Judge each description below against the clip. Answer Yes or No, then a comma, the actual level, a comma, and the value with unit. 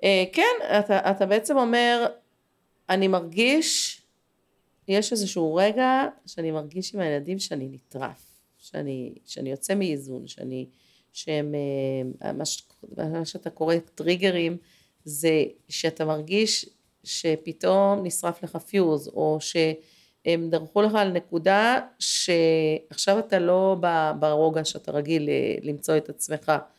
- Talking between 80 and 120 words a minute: Yes, average, 110 wpm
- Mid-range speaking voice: Yes, medium, 170 Hz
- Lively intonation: No, average, 4.1 semitones